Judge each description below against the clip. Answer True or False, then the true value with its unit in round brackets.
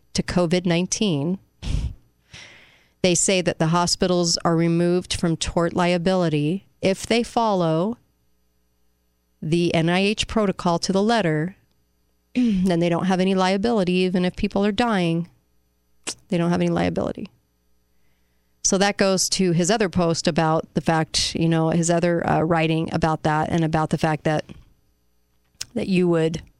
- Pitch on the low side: False (170 Hz)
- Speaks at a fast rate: False (140 wpm)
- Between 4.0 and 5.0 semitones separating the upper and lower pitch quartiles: False (3.0 semitones)